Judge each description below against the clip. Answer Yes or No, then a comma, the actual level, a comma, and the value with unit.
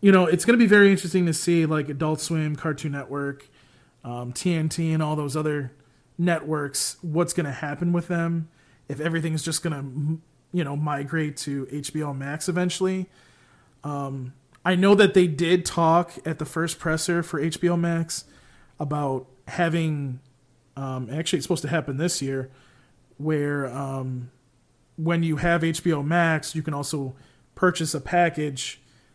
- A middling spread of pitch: Yes, average, 3.4 semitones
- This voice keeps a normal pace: Yes, average, 160 wpm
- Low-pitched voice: No, medium, 155 Hz